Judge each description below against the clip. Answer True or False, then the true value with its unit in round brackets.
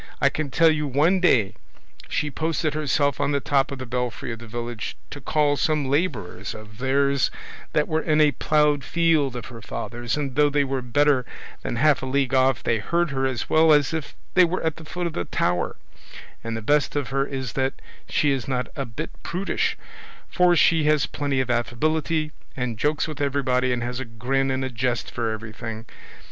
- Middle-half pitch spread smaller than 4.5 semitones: True (3.7 semitones)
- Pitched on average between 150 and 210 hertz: False (135 Hz)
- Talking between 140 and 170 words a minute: False (205 wpm)